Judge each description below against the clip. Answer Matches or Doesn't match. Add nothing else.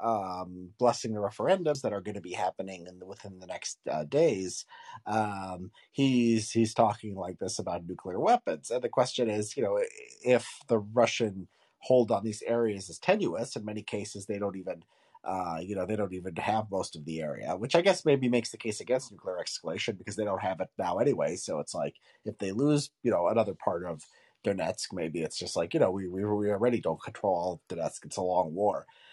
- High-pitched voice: Doesn't match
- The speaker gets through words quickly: Matches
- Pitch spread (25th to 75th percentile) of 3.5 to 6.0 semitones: Matches